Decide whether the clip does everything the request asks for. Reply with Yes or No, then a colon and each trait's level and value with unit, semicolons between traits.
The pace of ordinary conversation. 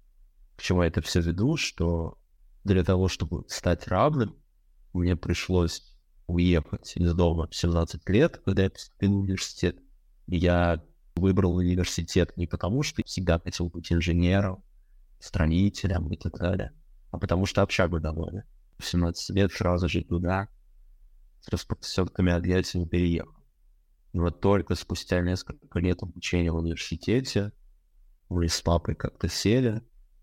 Yes: average, 135 wpm